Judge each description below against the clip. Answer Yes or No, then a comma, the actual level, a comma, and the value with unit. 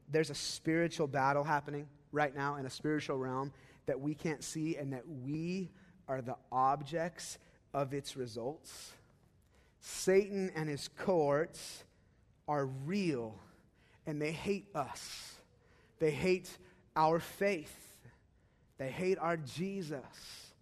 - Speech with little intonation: No, average, 3.7 semitones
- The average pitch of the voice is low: No, medium, 150 Hz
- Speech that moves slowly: Yes, slow, 120 wpm